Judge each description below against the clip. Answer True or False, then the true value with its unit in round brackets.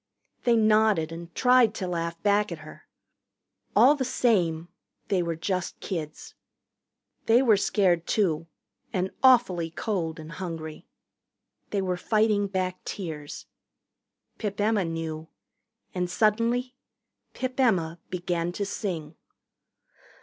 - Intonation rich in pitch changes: False (4.5 semitones)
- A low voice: False (185 Hz)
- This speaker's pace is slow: True (120 wpm)